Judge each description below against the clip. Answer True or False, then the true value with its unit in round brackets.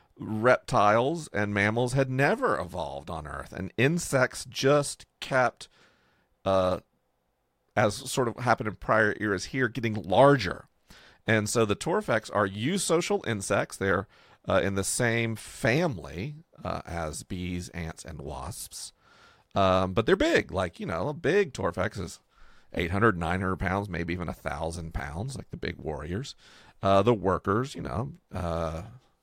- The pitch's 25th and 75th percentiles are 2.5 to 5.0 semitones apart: False (5.5 semitones)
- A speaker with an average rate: True (145 wpm)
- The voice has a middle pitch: False (105 Hz)